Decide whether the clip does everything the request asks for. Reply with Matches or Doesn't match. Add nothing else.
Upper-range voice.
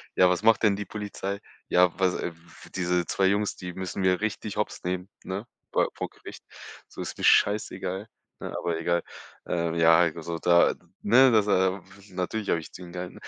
Doesn't match